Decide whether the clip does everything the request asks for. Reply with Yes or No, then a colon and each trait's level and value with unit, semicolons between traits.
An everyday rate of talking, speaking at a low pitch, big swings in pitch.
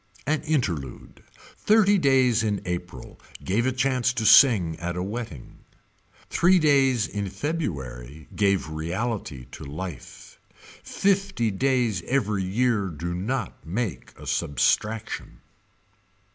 No: slow, 110 wpm; low, 105 Hz; wide, 6.9 semitones